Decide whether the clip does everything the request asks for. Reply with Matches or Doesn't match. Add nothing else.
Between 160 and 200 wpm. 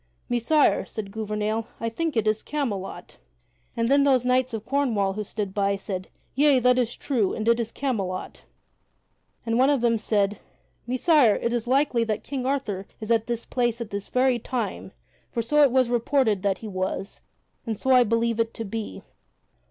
Matches